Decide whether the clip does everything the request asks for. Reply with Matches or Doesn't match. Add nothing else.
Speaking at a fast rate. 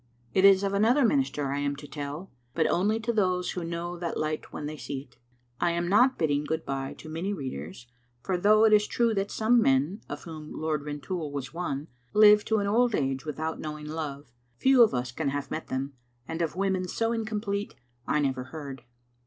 Matches